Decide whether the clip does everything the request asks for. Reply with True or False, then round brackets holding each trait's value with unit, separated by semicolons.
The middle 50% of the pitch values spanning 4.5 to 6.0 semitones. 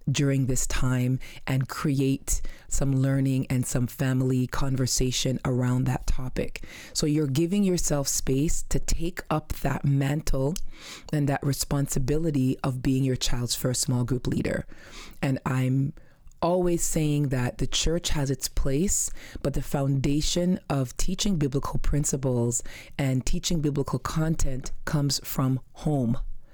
False (2.4 semitones)